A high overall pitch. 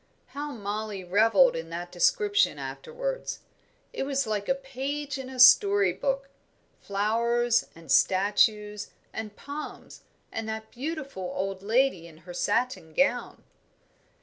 Yes: high, 225 Hz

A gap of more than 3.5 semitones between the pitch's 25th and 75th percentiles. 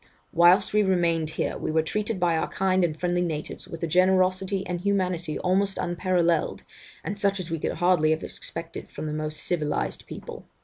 No: narrow, 2.6 semitones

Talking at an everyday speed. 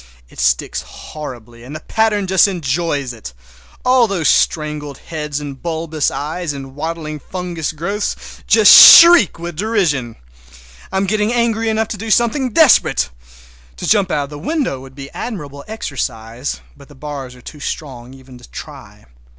Yes: average, 160 wpm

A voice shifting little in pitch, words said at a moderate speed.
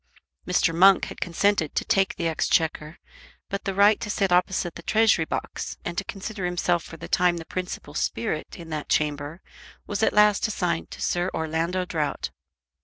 No: average, 3.4 semitones; average, 180 wpm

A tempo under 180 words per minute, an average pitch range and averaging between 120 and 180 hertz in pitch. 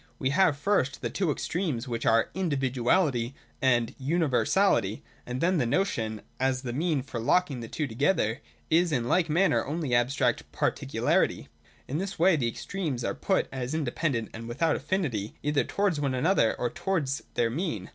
No: average, 165 wpm; wide, 5.9 semitones; medium, 140 Hz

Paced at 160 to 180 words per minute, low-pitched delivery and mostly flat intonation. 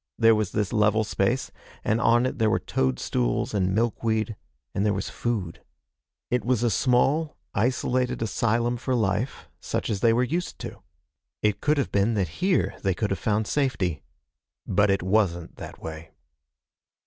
No: average, 165 wpm; low, 110 Hz; average, 3.8 semitones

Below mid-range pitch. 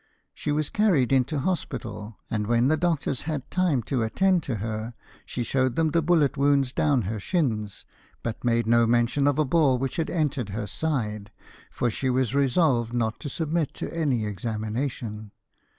Yes: low, 130 Hz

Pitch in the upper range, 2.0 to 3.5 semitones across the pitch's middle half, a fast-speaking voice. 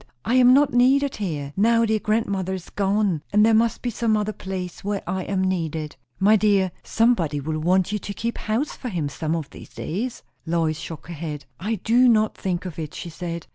No: high, 195 Hz; average, 4.8 semitones; fast, 215 wpm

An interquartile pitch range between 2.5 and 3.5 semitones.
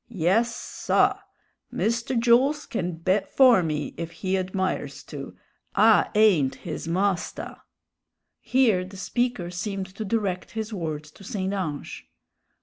No: average, 4.4 semitones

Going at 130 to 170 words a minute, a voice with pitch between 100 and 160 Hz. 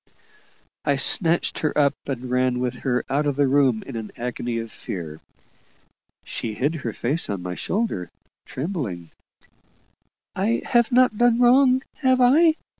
Yes: average, 150 wpm; medium, 140 Hz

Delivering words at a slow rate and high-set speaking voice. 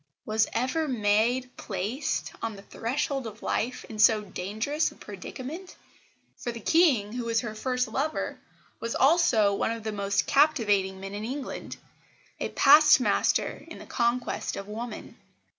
No: average, 155 wpm; high, 230 Hz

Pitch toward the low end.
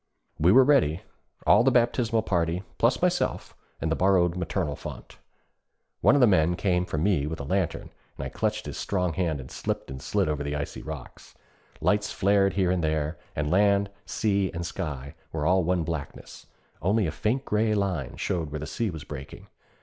Yes: very low, 90 Hz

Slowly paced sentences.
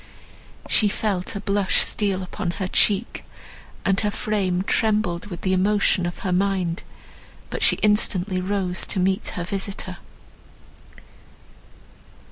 Yes: slow, 125 wpm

